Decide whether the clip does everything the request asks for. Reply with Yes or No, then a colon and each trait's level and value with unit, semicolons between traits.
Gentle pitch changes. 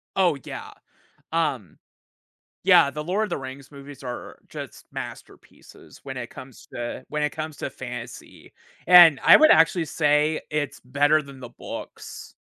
No: average, 3.2 semitones